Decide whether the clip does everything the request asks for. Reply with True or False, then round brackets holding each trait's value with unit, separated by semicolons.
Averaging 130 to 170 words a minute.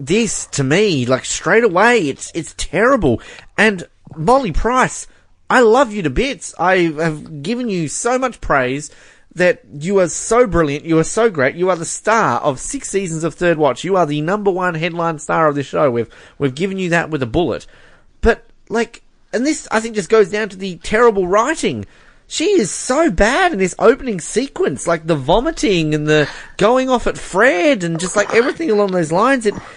False (200 wpm)